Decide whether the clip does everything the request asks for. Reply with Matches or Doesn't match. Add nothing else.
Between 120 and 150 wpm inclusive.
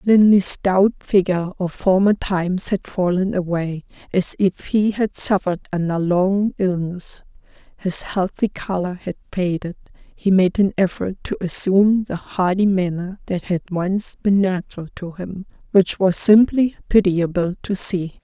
Matches